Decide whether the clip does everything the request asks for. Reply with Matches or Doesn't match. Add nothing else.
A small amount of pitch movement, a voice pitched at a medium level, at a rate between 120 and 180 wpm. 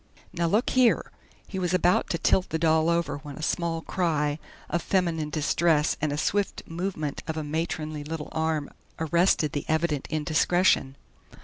Matches